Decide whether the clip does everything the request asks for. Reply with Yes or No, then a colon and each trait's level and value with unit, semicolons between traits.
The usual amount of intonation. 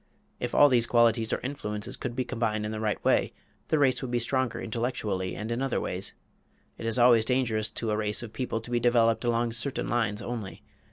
No: narrow, 2.1 semitones